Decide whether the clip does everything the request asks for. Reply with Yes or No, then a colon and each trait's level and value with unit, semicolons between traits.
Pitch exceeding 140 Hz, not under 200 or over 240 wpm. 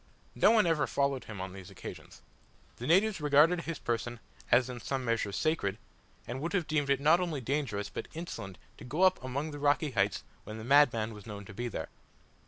No: low, 135 Hz; fast, 205 wpm